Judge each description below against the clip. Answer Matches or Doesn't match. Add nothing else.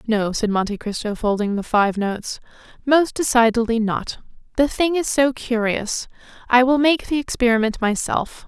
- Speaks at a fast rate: Doesn't match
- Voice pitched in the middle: Doesn't match